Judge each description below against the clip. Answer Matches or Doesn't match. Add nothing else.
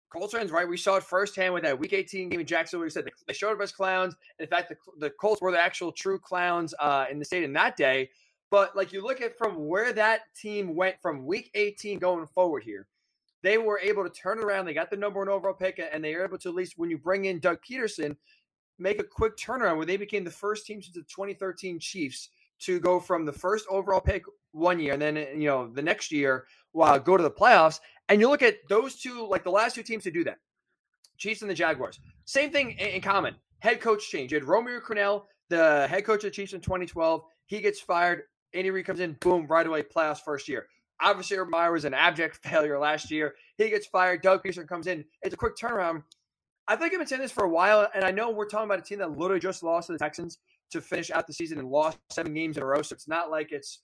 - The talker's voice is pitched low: Doesn't match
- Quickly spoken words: Matches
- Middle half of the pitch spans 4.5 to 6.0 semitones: Doesn't match